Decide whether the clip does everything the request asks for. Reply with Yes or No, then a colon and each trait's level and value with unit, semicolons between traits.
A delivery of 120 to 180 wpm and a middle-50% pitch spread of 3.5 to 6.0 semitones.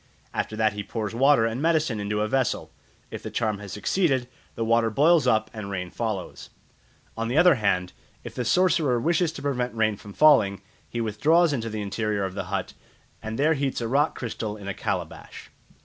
No: average, 195 wpm; average, 5.0 semitones